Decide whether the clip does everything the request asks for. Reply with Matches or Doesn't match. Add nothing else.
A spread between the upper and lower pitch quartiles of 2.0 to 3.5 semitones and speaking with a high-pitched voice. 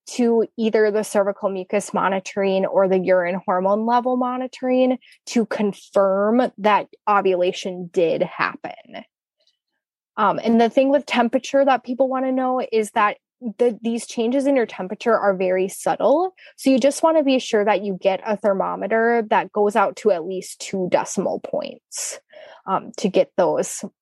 Doesn't match